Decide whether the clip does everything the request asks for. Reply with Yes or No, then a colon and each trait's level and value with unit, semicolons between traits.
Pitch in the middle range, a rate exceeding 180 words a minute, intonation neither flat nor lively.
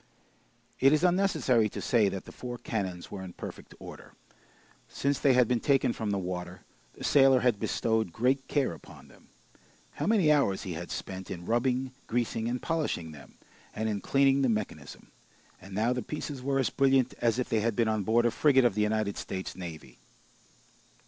No: low, 120 Hz; average, 190 wpm; average, 5.0 semitones